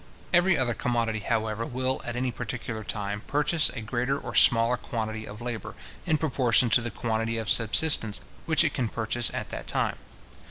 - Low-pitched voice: Yes, low, 120 Hz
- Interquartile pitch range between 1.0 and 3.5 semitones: Yes, average, 2.7 semitones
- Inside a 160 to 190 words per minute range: Yes, average, 175 wpm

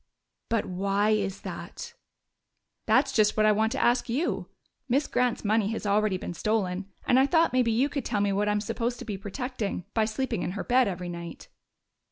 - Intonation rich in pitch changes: No, average, 3.7 semitones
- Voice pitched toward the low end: No, high, 215 Hz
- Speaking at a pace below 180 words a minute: No, average, 200 wpm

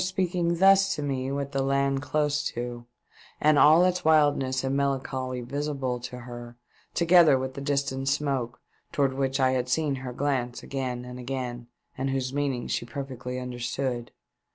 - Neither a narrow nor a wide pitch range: No, narrow, 2.3 semitones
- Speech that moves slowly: No, average, 160 wpm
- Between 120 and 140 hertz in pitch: Yes, low, 135 Hz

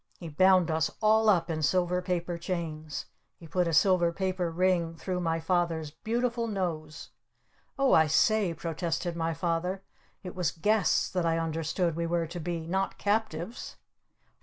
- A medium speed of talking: Yes, average, 160 wpm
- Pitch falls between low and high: Yes, medium, 175 Hz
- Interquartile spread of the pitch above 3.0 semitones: No, narrow, 2.4 semitones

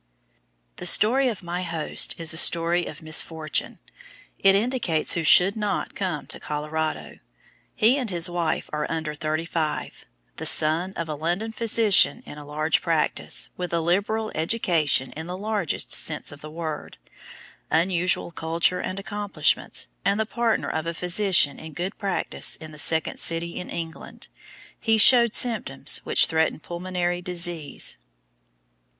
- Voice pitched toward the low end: No, medium, 170 Hz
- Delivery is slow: No, average, 150 wpm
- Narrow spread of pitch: No, average, 3.8 semitones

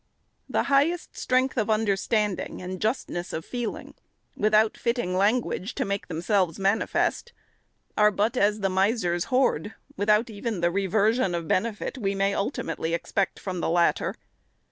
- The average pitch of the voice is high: Yes, high, 205 Hz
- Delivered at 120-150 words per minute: Yes, average, 145 wpm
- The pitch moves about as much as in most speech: Yes, average, 3.3 semitones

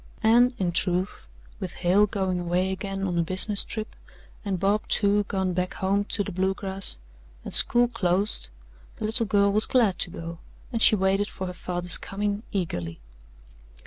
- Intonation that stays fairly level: Yes, narrow, 2.3 semitones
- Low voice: No, high, 195 Hz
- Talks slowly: No, average, 170 wpm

